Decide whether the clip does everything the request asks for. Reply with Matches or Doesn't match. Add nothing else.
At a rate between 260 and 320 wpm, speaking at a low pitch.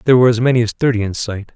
Matches